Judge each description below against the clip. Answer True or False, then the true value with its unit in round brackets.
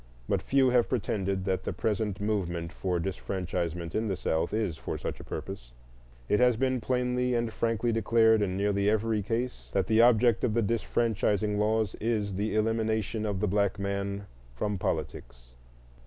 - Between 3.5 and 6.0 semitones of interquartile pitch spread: False (2.7 semitones)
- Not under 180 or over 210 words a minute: False (170 wpm)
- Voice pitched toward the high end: False (105 Hz)